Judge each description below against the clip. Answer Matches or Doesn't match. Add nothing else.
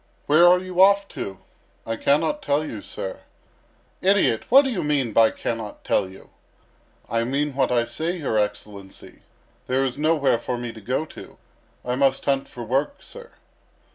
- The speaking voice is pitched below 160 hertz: Matches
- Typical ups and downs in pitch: Doesn't match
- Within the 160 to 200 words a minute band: Matches